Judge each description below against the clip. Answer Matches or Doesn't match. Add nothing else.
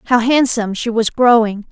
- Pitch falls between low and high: Doesn't match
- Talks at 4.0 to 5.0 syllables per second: Doesn't match